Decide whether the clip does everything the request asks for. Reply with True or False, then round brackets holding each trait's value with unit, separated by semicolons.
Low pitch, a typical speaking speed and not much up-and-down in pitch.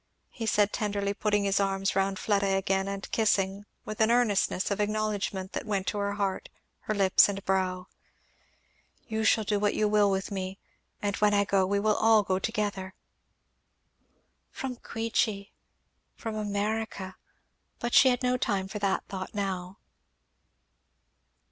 False (200 Hz; 155 wpm; 1.7 semitones)